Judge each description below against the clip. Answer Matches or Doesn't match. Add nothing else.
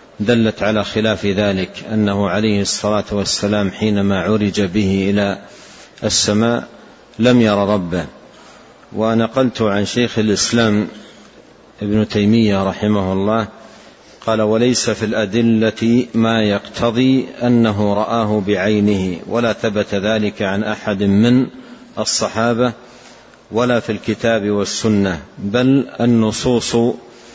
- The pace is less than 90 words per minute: Doesn't match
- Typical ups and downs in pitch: Doesn't match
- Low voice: Matches